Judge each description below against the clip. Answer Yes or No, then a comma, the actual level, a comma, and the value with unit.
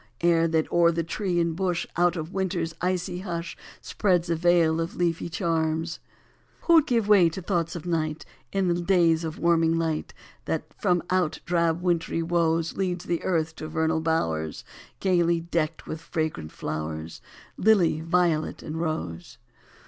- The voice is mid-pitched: Yes, medium, 170 Hz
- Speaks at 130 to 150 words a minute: No, average, 165 wpm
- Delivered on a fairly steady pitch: Yes, narrow, 1.7 semitones